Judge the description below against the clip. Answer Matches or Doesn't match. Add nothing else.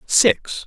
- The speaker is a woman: Doesn't match